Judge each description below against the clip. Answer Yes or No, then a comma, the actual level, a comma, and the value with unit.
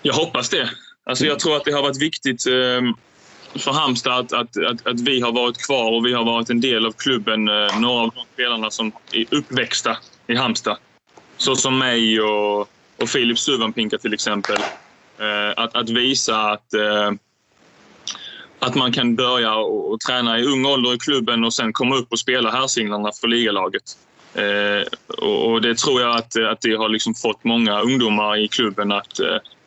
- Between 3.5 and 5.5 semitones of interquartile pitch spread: No, narrow, 2.5 semitones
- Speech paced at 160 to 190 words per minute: Yes, average, 170 wpm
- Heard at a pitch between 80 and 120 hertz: Yes, low, 115 Hz